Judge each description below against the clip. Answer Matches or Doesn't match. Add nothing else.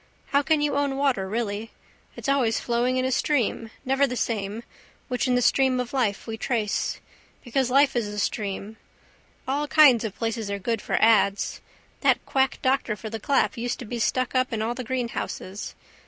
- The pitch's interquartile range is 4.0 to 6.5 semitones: Doesn't match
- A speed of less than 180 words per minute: Doesn't match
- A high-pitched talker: Matches